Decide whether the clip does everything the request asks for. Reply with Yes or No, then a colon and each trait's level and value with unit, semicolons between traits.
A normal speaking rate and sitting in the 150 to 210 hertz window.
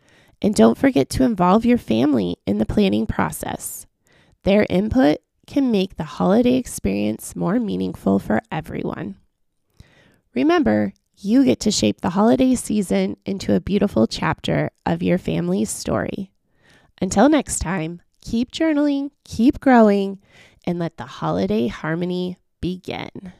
No: slow, 130 wpm; medium, 185 Hz